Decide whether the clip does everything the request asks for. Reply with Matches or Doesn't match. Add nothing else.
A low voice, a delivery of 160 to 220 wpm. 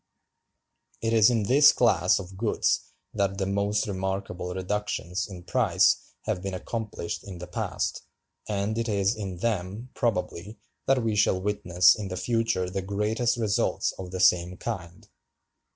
Doesn't match